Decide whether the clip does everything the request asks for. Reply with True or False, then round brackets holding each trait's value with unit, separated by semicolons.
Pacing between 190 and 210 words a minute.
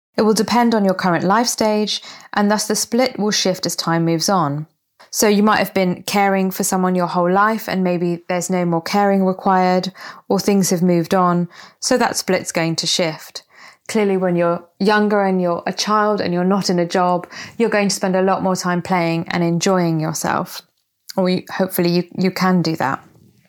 True (205 wpm)